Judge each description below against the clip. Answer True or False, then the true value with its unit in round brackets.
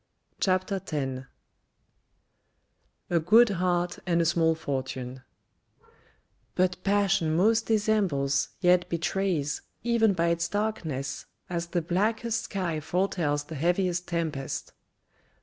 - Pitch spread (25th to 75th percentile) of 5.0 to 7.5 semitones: False (3.9 semitones)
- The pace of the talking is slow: True (105 wpm)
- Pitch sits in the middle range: True (175 Hz)